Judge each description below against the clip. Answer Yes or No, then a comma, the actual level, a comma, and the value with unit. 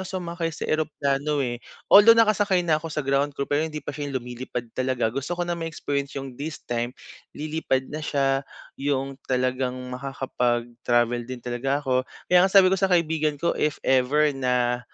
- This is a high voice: No, medium, 140 Hz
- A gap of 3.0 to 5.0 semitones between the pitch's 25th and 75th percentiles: Yes, average, 3.7 semitones